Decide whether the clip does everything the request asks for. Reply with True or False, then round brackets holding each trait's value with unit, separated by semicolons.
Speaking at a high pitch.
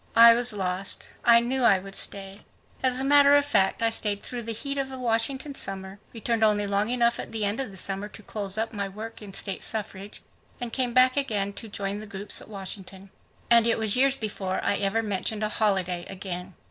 True (215 Hz)